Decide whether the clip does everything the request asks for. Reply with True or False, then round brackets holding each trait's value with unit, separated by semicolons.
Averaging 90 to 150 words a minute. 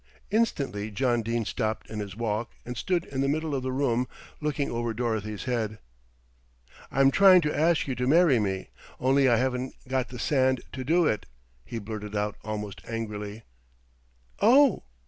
False (165 wpm)